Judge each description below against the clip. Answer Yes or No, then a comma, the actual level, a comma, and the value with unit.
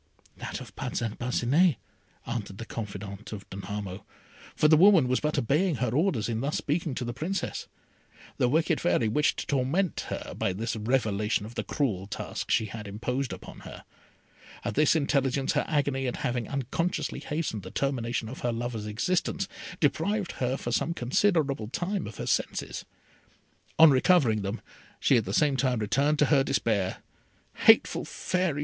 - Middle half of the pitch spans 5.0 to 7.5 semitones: Yes, wide, 5.4 semitones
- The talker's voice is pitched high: No, low, 130 Hz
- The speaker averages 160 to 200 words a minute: Yes, average, 170 wpm